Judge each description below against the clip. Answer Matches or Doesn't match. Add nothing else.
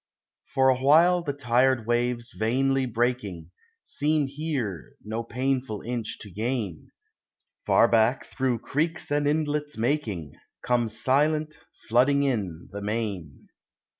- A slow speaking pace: Matches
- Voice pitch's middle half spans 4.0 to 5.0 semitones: Matches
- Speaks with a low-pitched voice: Matches